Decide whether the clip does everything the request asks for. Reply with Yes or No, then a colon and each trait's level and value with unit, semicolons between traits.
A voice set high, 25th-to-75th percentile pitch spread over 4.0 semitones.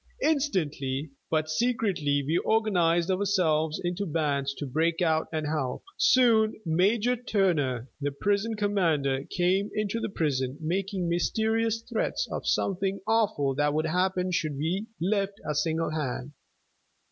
No: medium, 175 Hz; average, 5.1 semitones